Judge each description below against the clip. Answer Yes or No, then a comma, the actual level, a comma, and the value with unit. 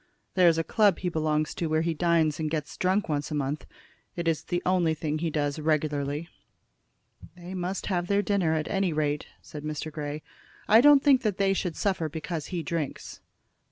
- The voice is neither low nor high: Yes, medium, 165 Hz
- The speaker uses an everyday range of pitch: Yes, average, 3.1 semitones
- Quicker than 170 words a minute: Yes, average, 190 wpm